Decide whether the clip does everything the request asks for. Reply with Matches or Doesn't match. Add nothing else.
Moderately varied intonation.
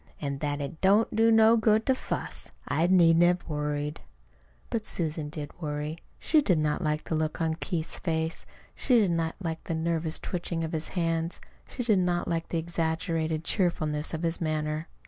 Doesn't match